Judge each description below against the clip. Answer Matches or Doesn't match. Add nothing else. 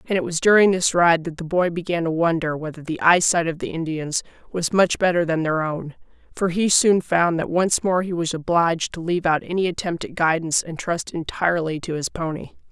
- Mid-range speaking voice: Matches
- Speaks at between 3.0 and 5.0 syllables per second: Doesn't match